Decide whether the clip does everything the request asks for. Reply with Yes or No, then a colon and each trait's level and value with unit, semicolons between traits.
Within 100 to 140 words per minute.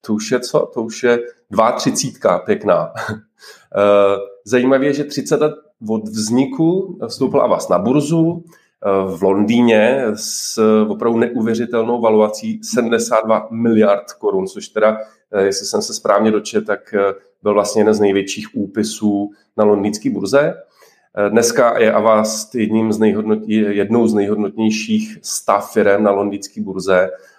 Yes: average, 130 wpm